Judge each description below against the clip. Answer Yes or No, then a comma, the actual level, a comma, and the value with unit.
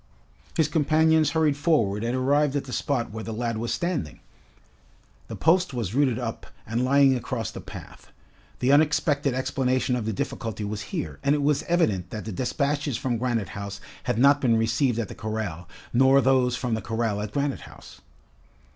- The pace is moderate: Yes, average, 180 wpm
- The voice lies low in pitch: Yes, low, 125 Hz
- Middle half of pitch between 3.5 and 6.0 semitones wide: Yes, average, 4.3 semitones